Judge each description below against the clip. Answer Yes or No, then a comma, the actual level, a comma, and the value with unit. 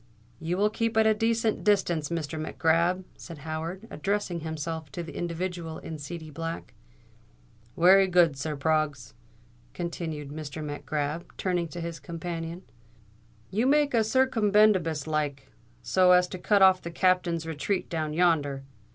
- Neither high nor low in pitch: Yes, medium, 170 Hz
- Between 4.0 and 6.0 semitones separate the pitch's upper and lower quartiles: No, average, 3.1 semitones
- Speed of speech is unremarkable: Yes, average, 150 wpm